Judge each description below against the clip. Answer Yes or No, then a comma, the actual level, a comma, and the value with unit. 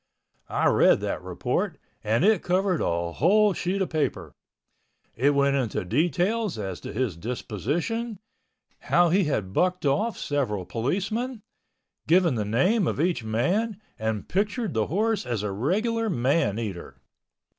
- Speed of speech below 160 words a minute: Yes, average, 145 wpm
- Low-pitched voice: No, medium, 155 Hz